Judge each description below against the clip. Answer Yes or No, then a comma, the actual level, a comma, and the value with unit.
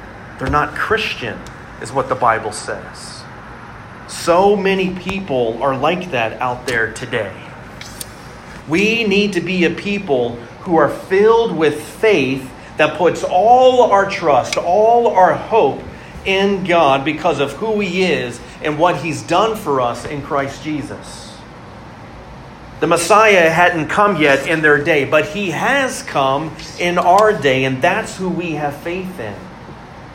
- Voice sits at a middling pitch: Yes, medium, 170 Hz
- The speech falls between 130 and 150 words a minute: Yes, average, 145 wpm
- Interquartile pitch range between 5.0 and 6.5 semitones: Yes, wide, 5.6 semitones